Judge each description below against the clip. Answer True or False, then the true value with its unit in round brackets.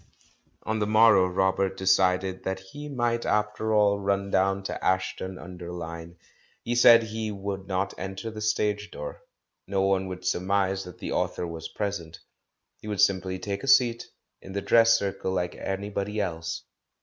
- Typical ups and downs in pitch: False (2.2 semitones)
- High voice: False (95 Hz)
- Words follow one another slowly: False (165 wpm)